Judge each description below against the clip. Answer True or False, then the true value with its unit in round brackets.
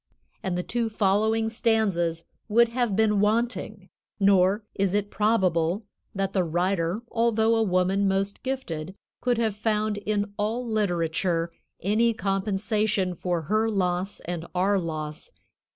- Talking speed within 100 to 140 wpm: True (135 wpm)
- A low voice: False (200 Hz)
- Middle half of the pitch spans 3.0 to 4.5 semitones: True (3.3 semitones)